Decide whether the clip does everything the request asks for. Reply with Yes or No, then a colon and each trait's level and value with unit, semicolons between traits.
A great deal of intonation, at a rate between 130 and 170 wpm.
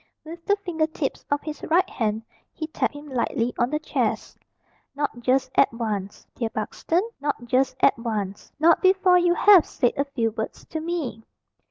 No: wide, 5.8 semitones; average, 180 wpm